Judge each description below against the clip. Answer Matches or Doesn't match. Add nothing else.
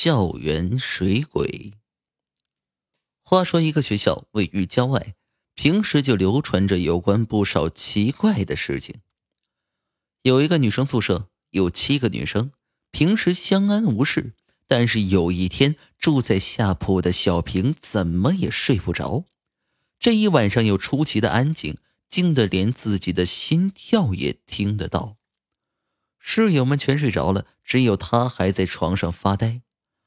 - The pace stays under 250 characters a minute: Matches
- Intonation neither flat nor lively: Doesn't match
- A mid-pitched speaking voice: Doesn't match